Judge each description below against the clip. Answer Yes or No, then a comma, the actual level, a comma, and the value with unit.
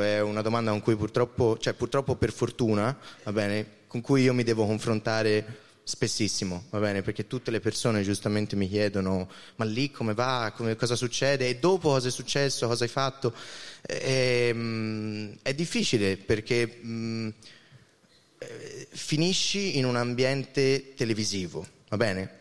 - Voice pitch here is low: Yes, low, 115 Hz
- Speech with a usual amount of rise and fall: Yes, average, 3.5 semitones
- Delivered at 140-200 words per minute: Yes, average, 145 wpm